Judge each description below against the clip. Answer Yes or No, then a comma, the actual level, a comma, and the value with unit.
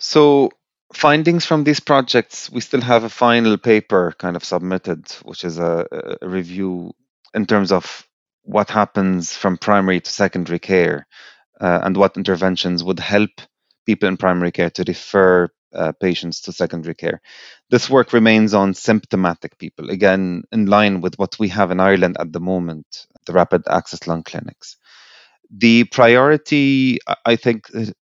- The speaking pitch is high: No, very low, 95 Hz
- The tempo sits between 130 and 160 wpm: Yes, average, 155 wpm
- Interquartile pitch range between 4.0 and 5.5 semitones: Yes, average, 4.5 semitones